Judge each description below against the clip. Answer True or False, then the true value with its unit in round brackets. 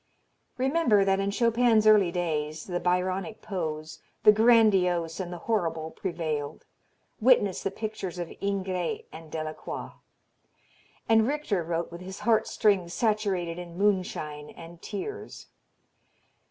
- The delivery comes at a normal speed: False (125 wpm)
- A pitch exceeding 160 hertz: True (185 Hz)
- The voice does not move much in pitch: False (4.1 semitones)